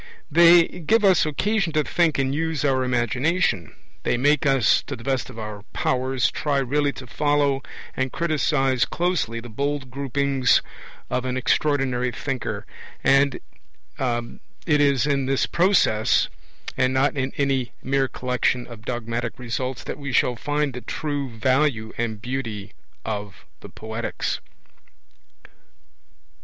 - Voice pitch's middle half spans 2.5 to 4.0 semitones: Yes, average, 3.1 semitones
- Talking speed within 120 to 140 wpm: Yes, slow, 135 wpm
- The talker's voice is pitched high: No, low, 135 Hz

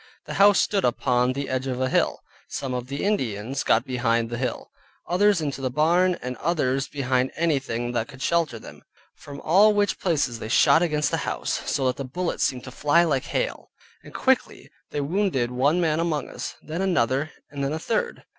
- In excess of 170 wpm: Yes, average, 200 wpm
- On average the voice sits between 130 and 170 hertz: Yes, medium, 140 Hz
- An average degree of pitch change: Yes, average, 5.0 semitones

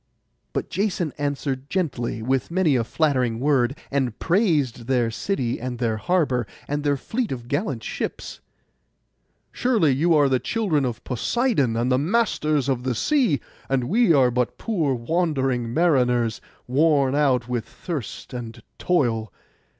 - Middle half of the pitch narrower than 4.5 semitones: No, average, 4.9 semitones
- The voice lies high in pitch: No, low, 135 Hz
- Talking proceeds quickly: No, average, 145 wpm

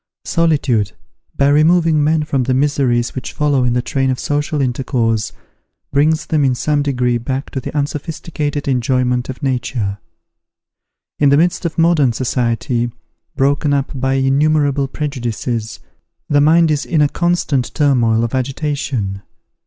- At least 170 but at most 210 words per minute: No, average, 145 wpm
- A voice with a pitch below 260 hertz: Yes, low, 135 Hz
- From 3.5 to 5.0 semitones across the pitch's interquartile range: No, average, 3.1 semitones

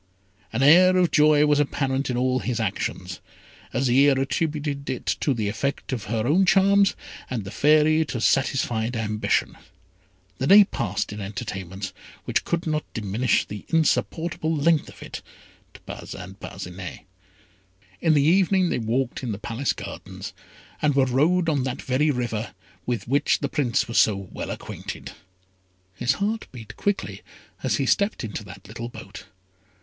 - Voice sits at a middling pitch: No, low, 130 Hz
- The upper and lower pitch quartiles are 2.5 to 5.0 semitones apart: No, wide, 5.6 semitones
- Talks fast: No, average, 155 wpm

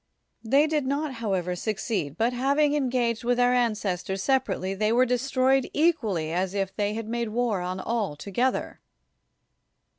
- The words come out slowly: No, average, 160 wpm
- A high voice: Yes, high, 230 Hz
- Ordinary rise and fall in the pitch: Yes, average, 4.8 semitones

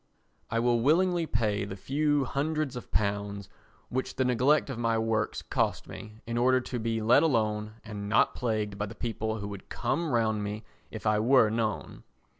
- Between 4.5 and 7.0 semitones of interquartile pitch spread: No, average, 3.3 semitones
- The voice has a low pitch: Yes, low, 115 Hz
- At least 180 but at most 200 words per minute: Yes, average, 185 wpm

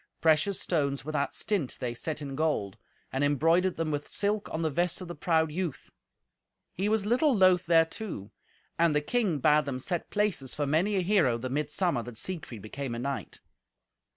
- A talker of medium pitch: Yes, medium, 160 Hz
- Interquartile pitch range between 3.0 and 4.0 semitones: No, average, 4.8 semitones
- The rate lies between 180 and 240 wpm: Yes, average, 185 wpm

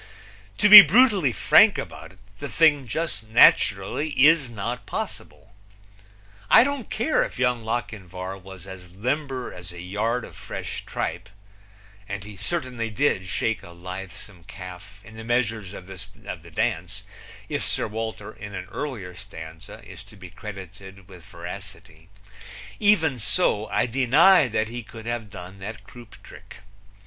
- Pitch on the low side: Yes, low, 105 Hz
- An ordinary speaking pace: Yes, average, 150 wpm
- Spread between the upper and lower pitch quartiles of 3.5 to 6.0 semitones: Yes, average, 4.7 semitones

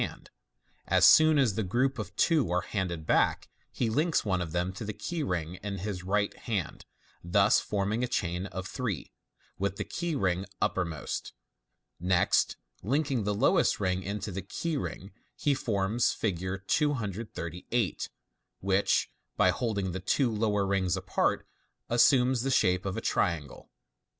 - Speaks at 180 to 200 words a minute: No, average, 150 wpm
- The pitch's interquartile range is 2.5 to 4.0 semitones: No, average, 4.6 semitones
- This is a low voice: Yes, low, 100 Hz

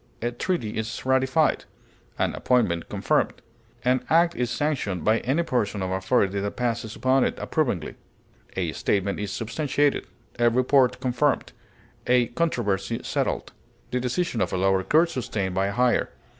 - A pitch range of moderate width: Yes, average, 4.6 semitones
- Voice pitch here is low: Yes, low, 120 Hz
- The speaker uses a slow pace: No, average, 150 wpm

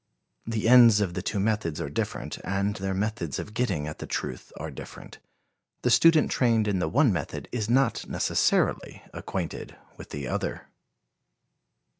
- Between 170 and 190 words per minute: No, average, 160 wpm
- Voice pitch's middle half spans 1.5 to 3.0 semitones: No, average, 4.1 semitones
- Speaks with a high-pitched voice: No, low, 105 Hz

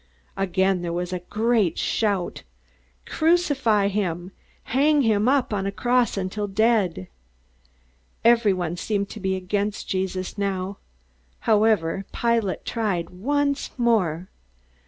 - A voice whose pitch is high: Yes, high, 200 Hz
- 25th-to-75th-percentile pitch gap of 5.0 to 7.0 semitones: No, average, 3.8 semitones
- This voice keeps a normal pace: No, slow, 120 wpm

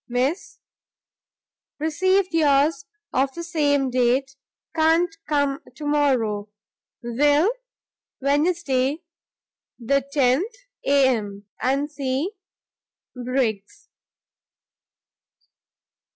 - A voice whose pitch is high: Yes, very high, 280 Hz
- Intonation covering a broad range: No, average, 3.7 semitones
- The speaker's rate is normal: No, slow, 65 wpm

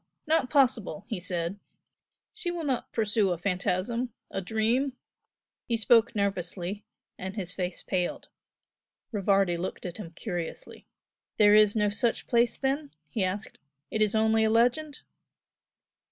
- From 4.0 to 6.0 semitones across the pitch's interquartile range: Yes, average, 4.3 semitones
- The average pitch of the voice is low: No, high, 215 Hz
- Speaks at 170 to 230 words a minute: No, average, 140 wpm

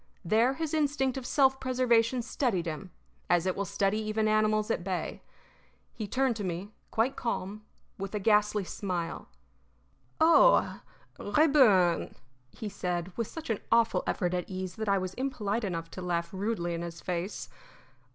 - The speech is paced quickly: No, average, 160 wpm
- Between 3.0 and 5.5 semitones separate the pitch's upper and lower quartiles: Yes, average, 4.7 semitones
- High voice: Yes, high, 210 Hz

